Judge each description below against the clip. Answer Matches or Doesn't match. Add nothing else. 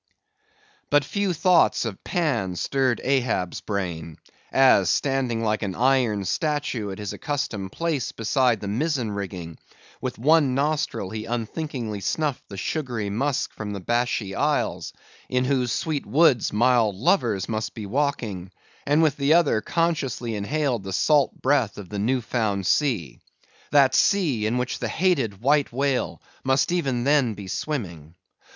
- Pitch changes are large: Matches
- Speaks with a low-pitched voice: Matches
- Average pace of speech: Matches